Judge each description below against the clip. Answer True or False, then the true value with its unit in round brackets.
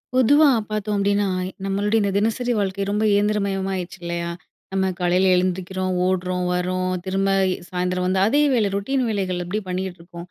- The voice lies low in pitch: False (190 Hz)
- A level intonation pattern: True (2.1 semitones)